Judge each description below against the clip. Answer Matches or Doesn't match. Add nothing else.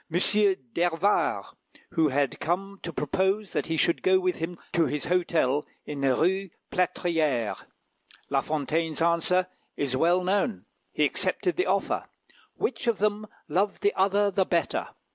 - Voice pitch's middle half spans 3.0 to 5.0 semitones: Matches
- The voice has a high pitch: Doesn't match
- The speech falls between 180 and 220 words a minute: Doesn't match